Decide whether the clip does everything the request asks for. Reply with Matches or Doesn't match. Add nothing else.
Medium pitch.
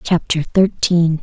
Matches